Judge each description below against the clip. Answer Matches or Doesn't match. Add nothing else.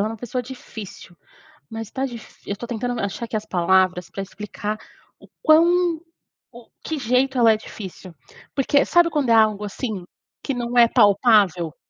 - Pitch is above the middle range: Matches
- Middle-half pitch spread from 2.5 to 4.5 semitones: Matches